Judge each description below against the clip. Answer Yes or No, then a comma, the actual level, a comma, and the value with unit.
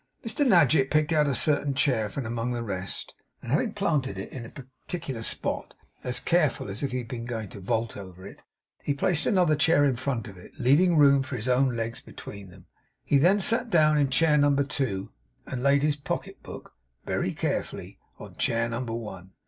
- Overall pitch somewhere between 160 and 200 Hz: No, low, 130 Hz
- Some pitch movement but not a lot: Yes, average, 4.7 semitones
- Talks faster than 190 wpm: Yes, average, 200 wpm